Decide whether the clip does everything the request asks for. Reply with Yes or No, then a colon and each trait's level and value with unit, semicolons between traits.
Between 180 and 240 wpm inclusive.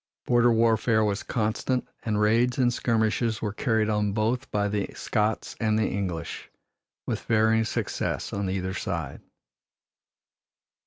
No: slow, 135 wpm